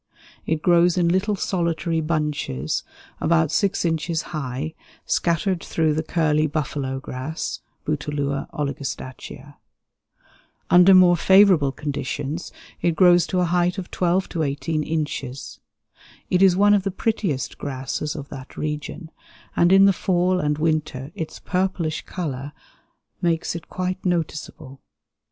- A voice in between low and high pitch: Yes, medium, 160 Hz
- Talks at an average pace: No, slow, 130 wpm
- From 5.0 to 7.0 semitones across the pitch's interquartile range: No, average, 3.4 semitones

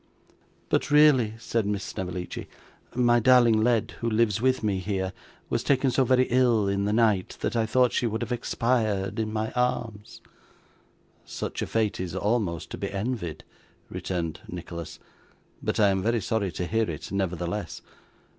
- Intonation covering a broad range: No, average, 3.8 semitones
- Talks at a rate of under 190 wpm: Yes, average, 165 wpm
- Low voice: Yes, low, 110 Hz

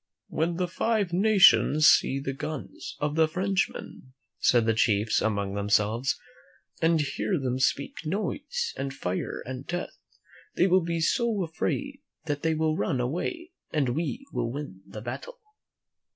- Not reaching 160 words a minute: Yes, average, 145 wpm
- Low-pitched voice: No, medium, 155 Hz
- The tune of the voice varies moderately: No, wide, 6.3 semitones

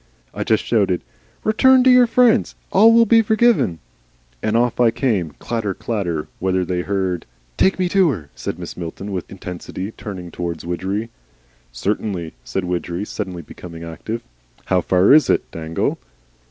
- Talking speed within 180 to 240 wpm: No, average, 160 wpm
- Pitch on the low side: Yes, very low, 95 Hz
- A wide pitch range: Yes, wide, 5.8 semitones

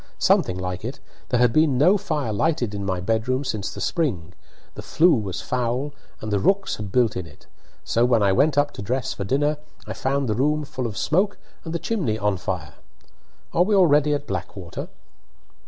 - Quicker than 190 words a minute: Yes, average, 200 wpm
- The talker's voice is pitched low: Yes, low, 125 Hz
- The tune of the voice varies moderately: No, wide, 6.7 semitones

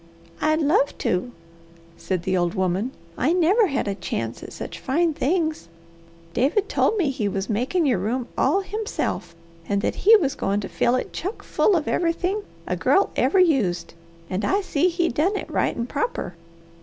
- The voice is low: No, very high, 285 Hz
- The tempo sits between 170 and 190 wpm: Yes, average, 180 wpm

